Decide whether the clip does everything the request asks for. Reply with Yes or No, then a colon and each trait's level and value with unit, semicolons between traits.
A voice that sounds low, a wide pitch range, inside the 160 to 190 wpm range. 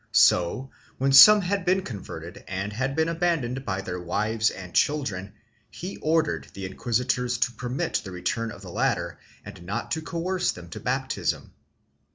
Yes: low, 125 Hz; wide, 8.6 semitones; average, 165 wpm